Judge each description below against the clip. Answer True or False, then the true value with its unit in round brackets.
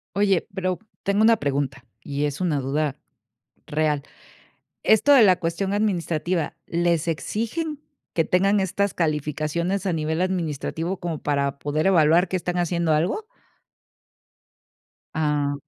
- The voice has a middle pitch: True (170 Hz)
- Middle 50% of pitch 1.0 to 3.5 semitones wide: False (4.1 semitones)